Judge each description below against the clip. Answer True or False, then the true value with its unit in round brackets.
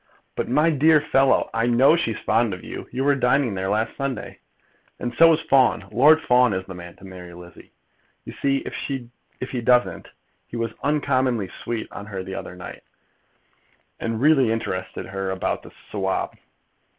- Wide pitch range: True (5.9 semitones)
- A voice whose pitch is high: False (120 Hz)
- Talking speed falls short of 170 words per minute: False (175 wpm)